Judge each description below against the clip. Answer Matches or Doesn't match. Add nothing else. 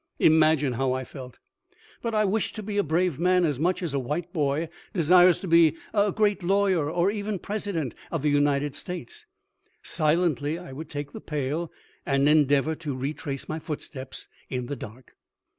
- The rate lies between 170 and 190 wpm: Matches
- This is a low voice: Doesn't match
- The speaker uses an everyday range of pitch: Matches